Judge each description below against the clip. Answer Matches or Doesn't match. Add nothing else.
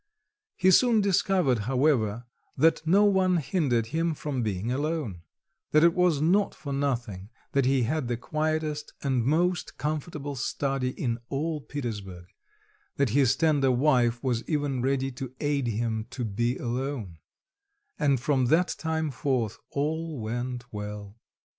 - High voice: Doesn't match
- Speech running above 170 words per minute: Doesn't match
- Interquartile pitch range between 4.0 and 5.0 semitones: Matches